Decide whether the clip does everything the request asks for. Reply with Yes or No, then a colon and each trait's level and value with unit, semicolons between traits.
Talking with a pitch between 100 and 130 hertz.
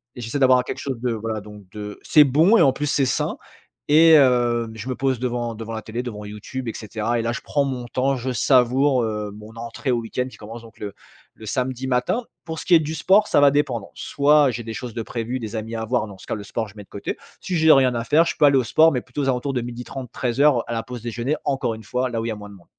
Yes: low, 120 Hz